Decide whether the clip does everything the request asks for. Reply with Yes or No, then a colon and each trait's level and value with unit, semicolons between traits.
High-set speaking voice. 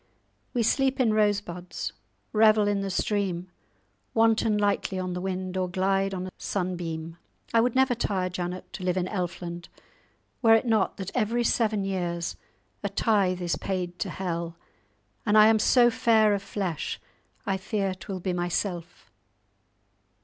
Yes: high, 195 Hz